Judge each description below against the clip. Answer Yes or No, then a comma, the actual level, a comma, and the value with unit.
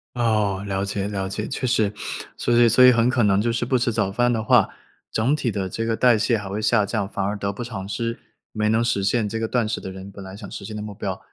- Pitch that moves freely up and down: No, average, 2.9 semitones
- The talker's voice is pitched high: No, low, 110 Hz